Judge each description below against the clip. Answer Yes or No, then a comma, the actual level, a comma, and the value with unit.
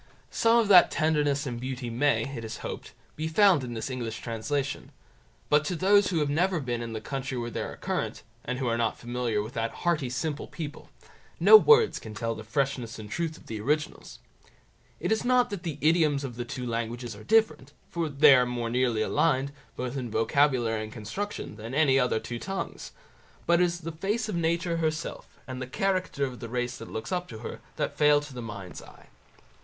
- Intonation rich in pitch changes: Yes, wide, 5.8 semitones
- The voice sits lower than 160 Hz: Yes, low, 135 Hz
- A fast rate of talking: Yes, fast, 210 wpm